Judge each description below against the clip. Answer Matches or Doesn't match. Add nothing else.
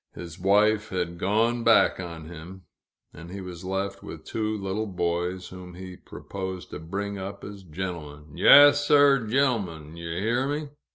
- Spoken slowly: Doesn't match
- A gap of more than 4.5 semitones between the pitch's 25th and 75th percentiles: Doesn't match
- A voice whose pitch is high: Doesn't match